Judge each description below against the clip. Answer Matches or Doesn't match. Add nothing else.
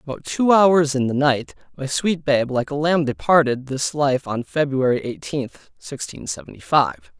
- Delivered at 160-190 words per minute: Matches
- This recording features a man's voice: Matches